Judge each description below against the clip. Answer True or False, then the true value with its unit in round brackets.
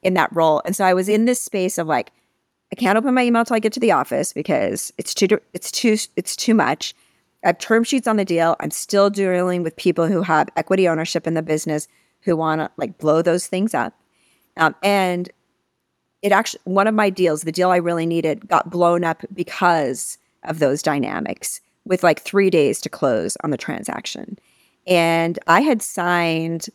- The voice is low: False (180 Hz)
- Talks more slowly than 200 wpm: False (205 wpm)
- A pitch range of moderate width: True (3.7 semitones)